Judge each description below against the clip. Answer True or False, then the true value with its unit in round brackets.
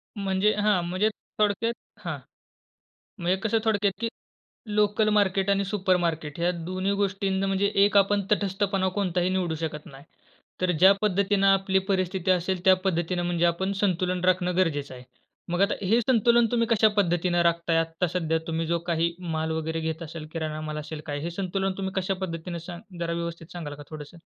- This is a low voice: False (185 Hz)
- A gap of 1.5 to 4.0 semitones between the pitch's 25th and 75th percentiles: True (2.9 semitones)